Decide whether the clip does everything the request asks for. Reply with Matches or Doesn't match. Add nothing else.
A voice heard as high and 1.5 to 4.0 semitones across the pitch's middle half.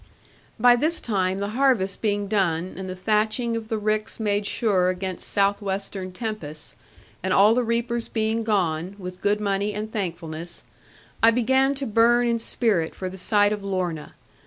Matches